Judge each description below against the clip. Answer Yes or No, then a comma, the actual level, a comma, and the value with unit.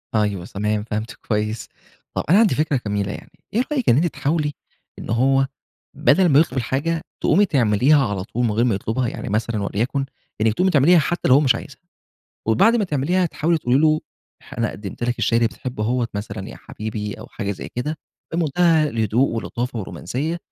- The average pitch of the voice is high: No, low, 125 Hz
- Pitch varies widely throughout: Yes, wide, 6.1 semitones